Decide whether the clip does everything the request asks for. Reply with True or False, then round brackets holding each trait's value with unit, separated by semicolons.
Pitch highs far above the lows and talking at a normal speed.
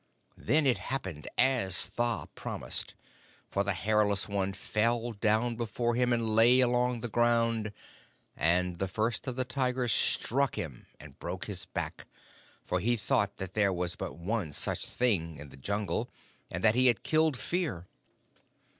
False (4.3 semitones; 160 wpm)